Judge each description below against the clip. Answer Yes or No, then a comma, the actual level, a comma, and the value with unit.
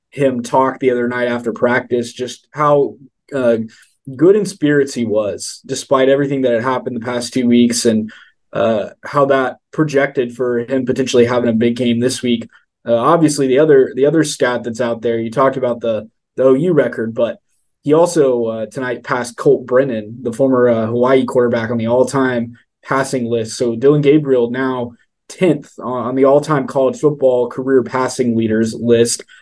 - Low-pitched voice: Yes, low, 125 Hz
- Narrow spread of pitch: Yes, narrow, 2.2 semitones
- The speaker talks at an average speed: Yes, average, 180 wpm